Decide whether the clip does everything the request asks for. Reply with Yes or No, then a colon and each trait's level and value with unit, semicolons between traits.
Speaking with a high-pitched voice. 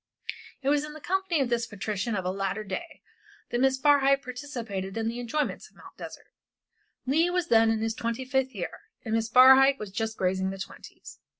Yes: high, 240 Hz